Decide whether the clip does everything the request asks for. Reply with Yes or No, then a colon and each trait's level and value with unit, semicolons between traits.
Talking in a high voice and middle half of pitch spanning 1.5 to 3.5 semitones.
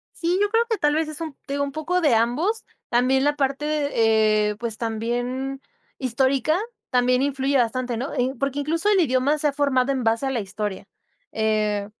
No: very high, 265 Hz; average, 4.0 semitones